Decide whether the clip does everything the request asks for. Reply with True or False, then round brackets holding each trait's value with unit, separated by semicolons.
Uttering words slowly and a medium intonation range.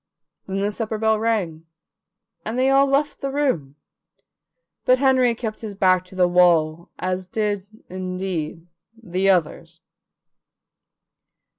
True (125 wpm; 4.3 semitones)